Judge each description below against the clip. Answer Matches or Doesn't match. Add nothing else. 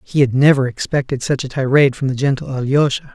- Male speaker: Matches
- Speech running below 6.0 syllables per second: Doesn't match